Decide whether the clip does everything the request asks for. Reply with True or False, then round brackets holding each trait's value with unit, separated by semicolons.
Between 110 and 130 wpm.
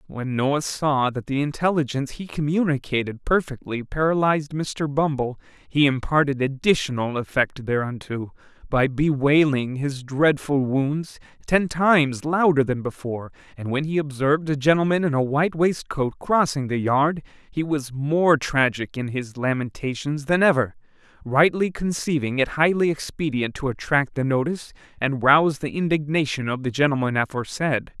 False (140 wpm)